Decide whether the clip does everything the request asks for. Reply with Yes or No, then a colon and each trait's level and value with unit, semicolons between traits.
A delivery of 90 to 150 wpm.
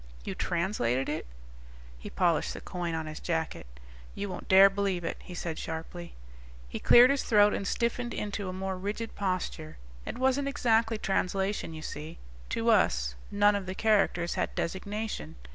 No: average, 165 wpm